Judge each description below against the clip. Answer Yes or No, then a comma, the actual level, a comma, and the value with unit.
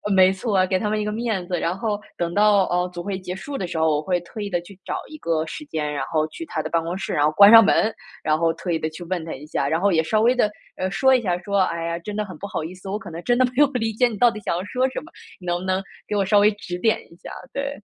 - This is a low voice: No, high, 190 Hz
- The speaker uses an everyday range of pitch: Yes, average, 4.0 semitones